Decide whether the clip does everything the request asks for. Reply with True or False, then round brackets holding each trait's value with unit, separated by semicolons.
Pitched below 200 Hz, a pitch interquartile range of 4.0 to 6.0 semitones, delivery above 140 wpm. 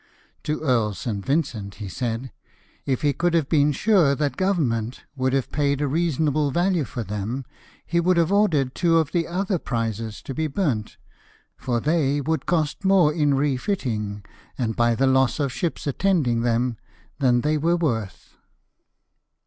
True (140 Hz; 5.3 semitones; 165 wpm)